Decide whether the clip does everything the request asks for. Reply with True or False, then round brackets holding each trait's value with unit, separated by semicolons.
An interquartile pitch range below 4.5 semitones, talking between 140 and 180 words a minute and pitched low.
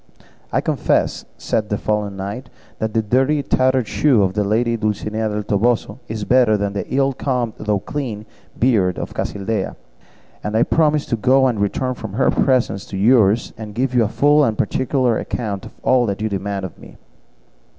False (3.7 semitones; 190 wpm; 110 Hz)